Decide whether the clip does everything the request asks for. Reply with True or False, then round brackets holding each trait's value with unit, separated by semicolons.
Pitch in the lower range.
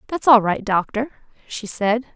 False (225 Hz)